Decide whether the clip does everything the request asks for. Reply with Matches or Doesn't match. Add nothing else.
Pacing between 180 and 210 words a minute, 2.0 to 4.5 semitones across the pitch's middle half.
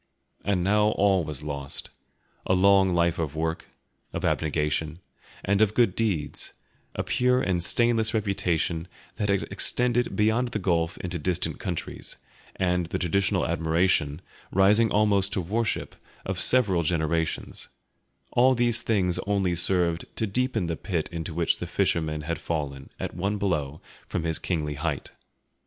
Doesn't match